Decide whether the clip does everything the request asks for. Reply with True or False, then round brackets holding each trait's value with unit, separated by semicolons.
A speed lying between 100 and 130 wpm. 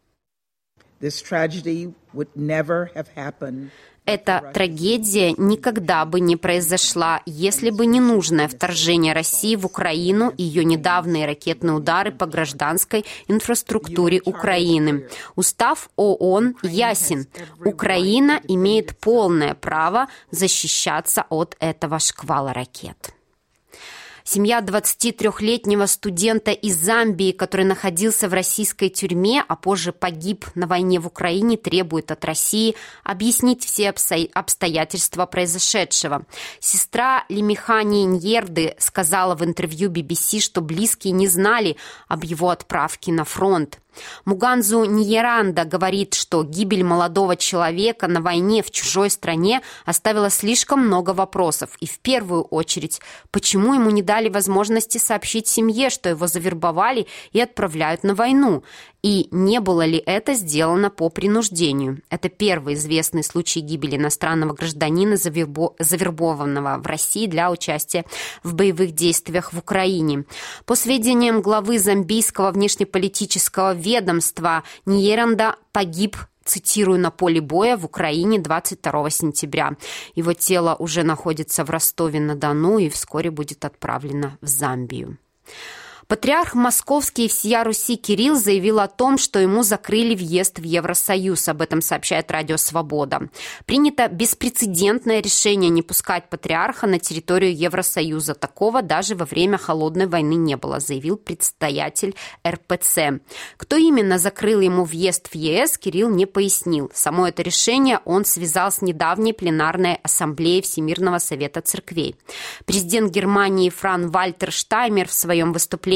True (120 wpm)